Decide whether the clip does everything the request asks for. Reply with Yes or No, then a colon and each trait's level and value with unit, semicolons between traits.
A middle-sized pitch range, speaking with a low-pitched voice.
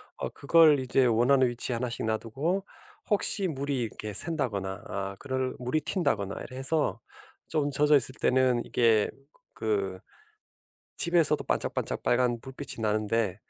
Yes: average, 4.5 semitones; low, 125 Hz